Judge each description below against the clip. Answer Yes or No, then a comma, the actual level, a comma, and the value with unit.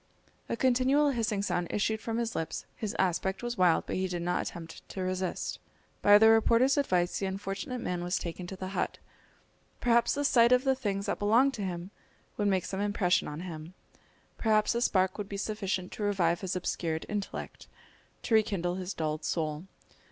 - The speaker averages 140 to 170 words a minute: No, average, 190 wpm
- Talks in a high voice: Yes, high, 195 Hz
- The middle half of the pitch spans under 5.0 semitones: Yes, average, 3.8 semitones